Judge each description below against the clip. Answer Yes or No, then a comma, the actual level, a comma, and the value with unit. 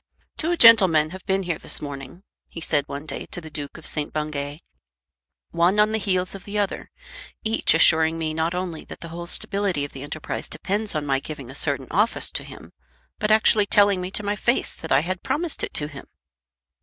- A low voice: No, medium, 170 Hz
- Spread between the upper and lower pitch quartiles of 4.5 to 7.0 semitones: Yes, average, 5.1 semitones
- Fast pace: Yes, fast, 210 wpm